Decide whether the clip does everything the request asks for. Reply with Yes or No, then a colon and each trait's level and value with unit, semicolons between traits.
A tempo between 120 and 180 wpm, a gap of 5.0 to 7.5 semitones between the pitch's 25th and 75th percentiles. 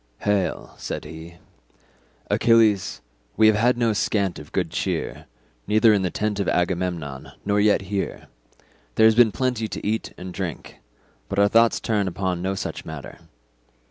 No: average, 160 wpm; average, 3.3 semitones